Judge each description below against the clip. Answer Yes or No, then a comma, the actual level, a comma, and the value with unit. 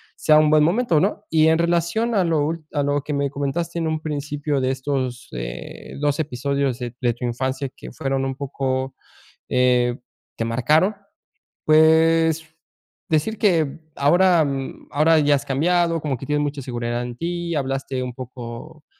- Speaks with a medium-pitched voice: Yes, medium, 145 Hz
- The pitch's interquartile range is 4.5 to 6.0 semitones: No, average, 3.6 semitones